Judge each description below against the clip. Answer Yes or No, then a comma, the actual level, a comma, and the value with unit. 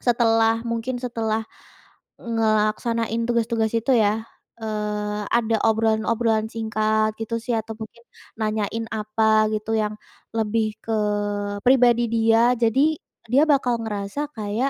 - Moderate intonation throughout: No, narrow, 1.3 semitones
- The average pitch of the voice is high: Yes, high, 225 Hz